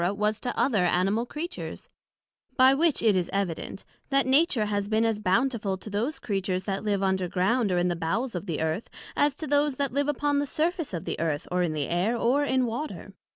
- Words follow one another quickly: Yes, fast, 210 wpm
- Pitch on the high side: Yes, high, 215 Hz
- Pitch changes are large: Yes, wide, 6.5 semitones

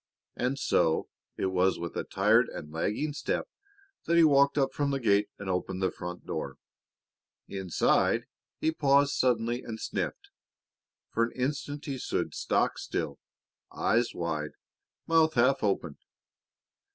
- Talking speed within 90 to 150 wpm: Yes, average, 140 wpm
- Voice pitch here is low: Yes, low, 120 Hz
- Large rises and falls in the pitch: Yes, wide, 6.9 semitones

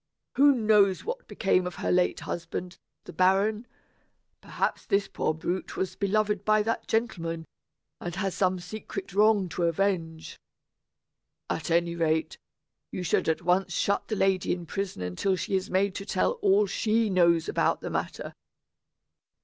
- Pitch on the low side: No, high, 190 Hz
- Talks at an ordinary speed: Yes, average, 155 wpm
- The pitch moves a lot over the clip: No, average, 3.0 semitones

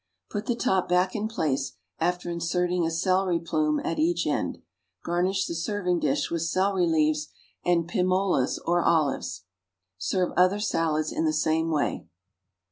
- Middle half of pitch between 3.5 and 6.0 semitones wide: No, narrow, 2.5 semitones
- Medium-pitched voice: Yes, medium, 170 Hz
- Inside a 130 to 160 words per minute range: Yes, average, 155 wpm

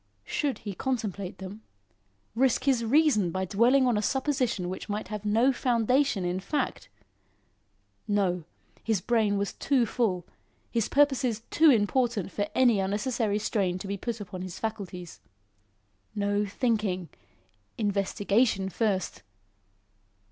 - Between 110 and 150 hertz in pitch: No, high, 210 Hz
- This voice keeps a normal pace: No, slow, 125 wpm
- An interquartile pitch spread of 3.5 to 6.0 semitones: Yes, average, 4.1 semitones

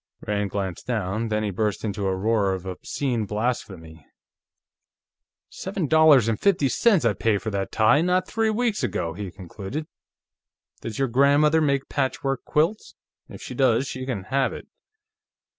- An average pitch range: No, wide, 6.0 semitones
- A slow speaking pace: No, average, 160 wpm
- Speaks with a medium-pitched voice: No, low, 115 Hz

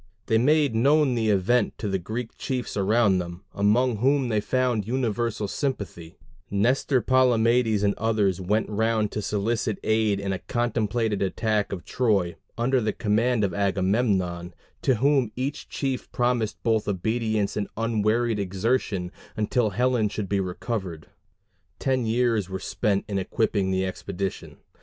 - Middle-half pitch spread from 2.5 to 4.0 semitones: Yes, average, 3.5 semitones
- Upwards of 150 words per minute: No, average, 145 wpm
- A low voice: Yes, low, 110 Hz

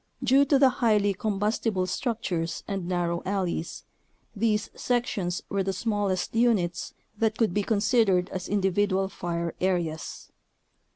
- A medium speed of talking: No, slow, 125 wpm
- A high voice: Yes, high, 195 Hz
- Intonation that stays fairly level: No, average, 3.6 semitones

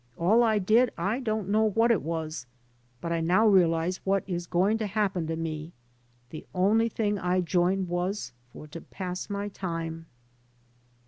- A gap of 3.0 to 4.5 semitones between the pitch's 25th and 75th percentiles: Yes, average, 3.9 semitones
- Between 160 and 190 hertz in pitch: Yes, medium, 185 Hz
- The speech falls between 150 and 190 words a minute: Yes, average, 170 wpm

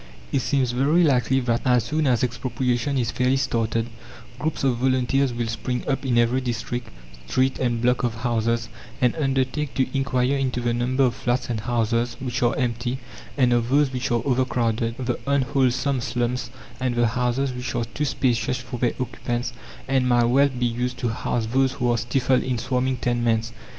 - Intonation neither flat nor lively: No, narrow, 1.7 semitones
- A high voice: No, low, 125 Hz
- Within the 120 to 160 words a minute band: No, average, 185 wpm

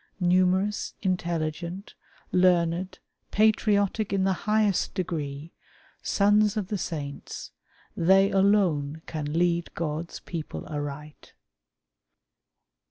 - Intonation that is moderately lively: Yes, average, 3.9 semitones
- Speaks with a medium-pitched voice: Yes, medium, 180 Hz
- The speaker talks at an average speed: No, slow, 90 wpm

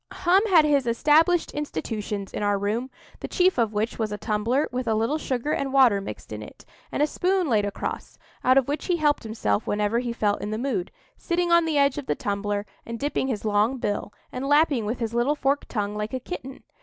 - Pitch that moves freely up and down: Yes, wide, 5.7 semitones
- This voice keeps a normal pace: No, fast, 220 wpm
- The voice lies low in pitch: No, high, 245 Hz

